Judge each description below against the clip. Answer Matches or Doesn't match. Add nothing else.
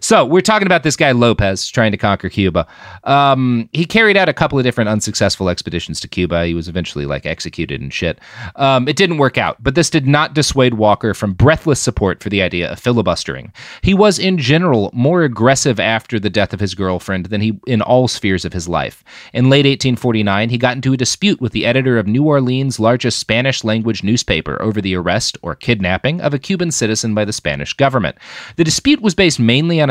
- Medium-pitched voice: Doesn't match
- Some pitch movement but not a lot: Doesn't match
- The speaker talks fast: Matches